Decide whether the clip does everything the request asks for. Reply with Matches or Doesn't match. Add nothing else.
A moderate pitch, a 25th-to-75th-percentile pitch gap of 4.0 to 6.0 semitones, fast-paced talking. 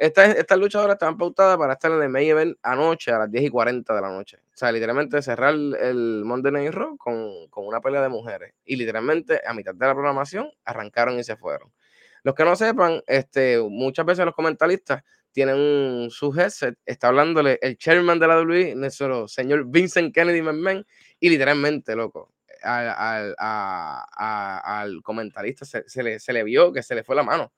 Matches